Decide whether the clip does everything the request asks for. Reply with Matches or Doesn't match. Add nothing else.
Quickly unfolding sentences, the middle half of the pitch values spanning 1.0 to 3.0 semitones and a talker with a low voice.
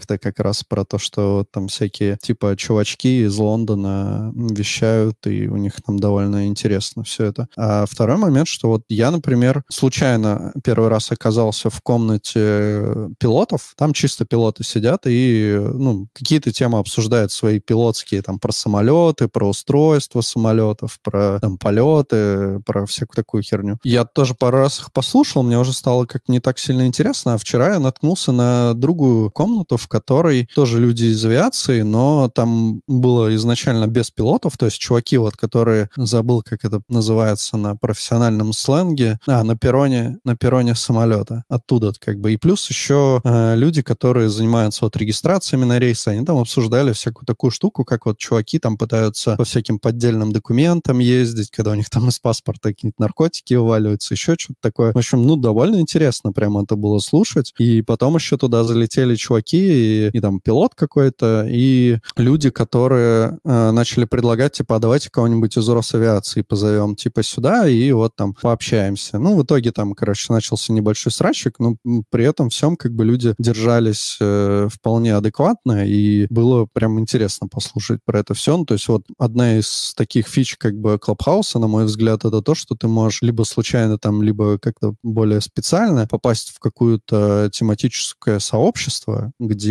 Matches